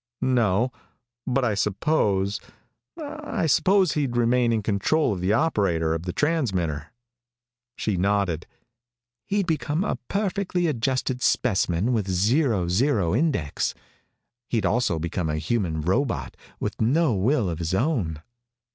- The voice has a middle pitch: No, low, 110 Hz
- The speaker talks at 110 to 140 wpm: Yes, slow, 135 wpm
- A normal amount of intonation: No, wide, 8.1 semitones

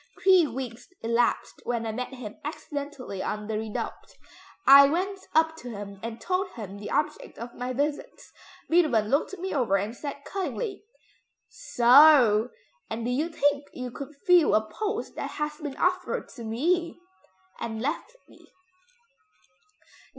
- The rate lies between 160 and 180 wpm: No, average, 150 wpm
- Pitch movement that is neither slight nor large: No, wide, 5.9 semitones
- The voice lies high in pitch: Yes, very high, 275 Hz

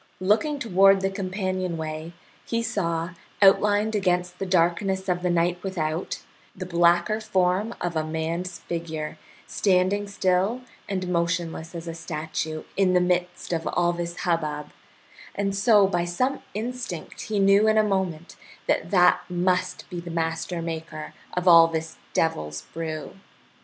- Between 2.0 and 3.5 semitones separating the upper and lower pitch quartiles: Yes, average, 2.8 semitones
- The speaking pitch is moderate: Yes, medium, 180 Hz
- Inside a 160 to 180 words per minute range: No, average, 145 wpm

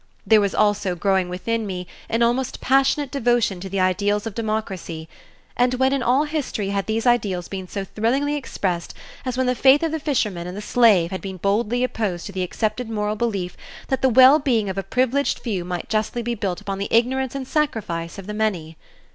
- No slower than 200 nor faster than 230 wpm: Yes, fast, 205 wpm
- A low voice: No, high, 215 Hz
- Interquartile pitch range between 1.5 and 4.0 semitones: No, average, 4.7 semitones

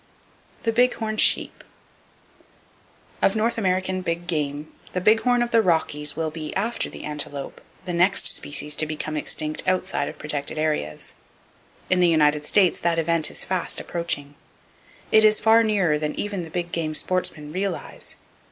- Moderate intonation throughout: Yes, average, 4.4 semitones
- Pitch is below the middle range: No, medium, 170 Hz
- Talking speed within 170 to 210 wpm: No, average, 160 wpm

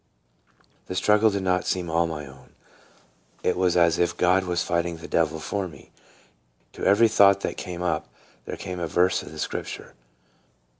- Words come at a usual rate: Yes, average, 180 wpm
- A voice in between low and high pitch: No, very low, 90 Hz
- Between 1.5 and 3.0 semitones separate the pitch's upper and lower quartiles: Yes, narrow, 2.4 semitones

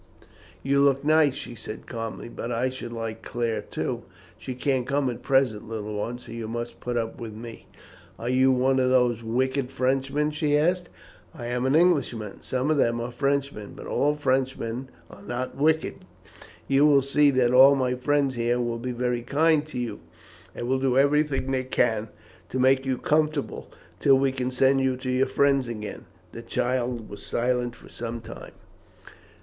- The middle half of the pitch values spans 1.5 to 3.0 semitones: Yes, narrow, 2.6 semitones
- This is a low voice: Yes, low, 130 Hz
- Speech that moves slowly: No, average, 185 wpm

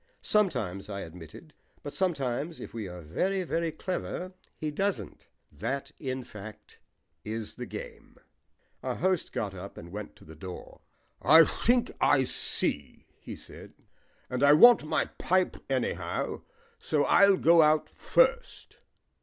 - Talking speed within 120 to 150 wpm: Yes, average, 140 wpm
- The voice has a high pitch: No, medium, 145 Hz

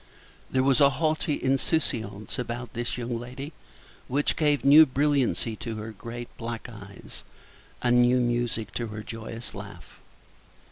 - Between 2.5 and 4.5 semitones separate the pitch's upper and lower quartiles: Yes, average, 3.1 semitones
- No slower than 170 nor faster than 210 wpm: No, average, 140 wpm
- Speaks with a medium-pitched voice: No, low, 120 Hz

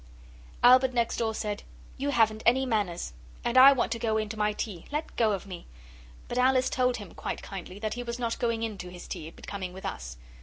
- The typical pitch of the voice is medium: No, high, 225 Hz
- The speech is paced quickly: Yes, fast, 230 wpm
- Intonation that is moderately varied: Yes, average, 3.5 semitones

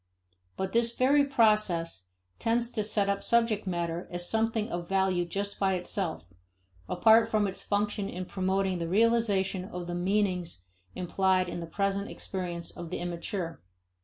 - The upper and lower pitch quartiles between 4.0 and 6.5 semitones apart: No, average, 3.3 semitones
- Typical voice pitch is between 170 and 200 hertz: Yes, high, 190 Hz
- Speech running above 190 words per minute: No, average, 155 wpm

